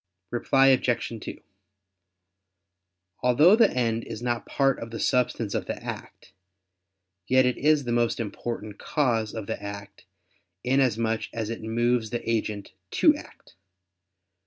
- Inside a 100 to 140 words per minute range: Yes, slow, 135 wpm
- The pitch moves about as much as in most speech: No, narrow, 2.2 semitones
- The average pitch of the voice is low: Yes, low, 120 Hz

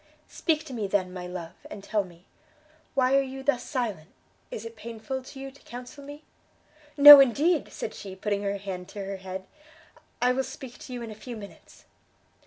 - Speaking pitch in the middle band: No, high, 230 Hz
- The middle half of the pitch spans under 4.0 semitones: No, wide, 5.4 semitones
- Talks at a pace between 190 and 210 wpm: Yes, average, 195 wpm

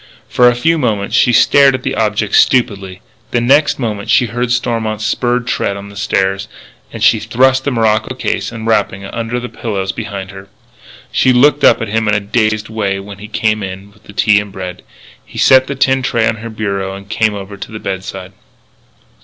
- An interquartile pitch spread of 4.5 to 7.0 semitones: No, average, 3.5 semitones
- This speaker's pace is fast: Yes, fast, 210 wpm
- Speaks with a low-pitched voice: Yes, low, 110 Hz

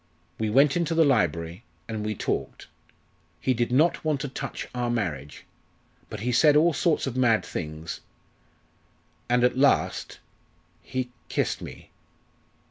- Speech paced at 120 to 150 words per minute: Yes, average, 140 wpm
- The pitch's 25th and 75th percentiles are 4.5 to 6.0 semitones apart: Yes, average, 5.0 semitones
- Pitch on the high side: No, low, 125 Hz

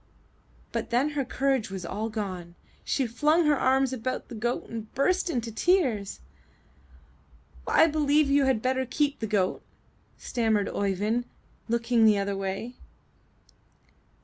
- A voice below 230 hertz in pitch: No, high, 240 Hz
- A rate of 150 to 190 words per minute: No, average, 140 wpm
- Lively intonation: No, average, 4.6 semitones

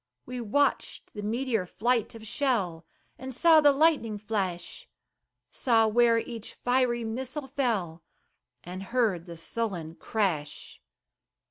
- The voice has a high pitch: Yes, high, 225 Hz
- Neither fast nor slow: No, slow, 120 wpm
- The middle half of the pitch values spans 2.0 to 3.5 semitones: No, average, 4.9 semitones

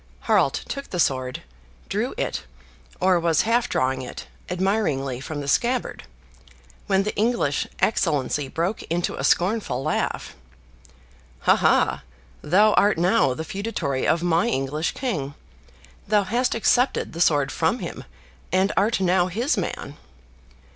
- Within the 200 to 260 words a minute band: No, slow, 135 wpm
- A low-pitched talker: No, medium, 175 Hz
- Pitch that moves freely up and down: Yes, wide, 6.8 semitones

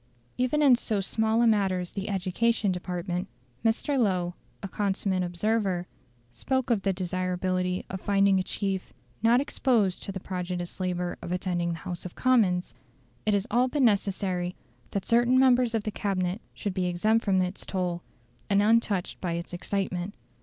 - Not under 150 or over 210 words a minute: Yes, average, 165 wpm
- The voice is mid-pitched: No, high, 195 Hz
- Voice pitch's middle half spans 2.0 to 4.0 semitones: Yes, average, 3.5 semitones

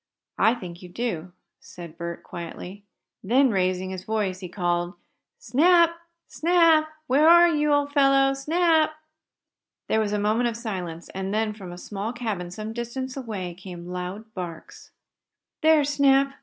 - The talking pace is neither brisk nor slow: Yes, average, 150 wpm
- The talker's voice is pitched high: Yes, high, 220 Hz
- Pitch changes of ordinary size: No, wide, 7.1 semitones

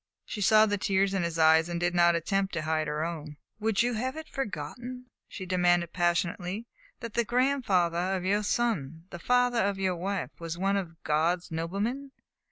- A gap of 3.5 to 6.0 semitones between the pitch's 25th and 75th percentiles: Yes, average, 4.5 semitones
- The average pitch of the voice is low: No, medium, 185 Hz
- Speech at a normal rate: Yes, average, 185 wpm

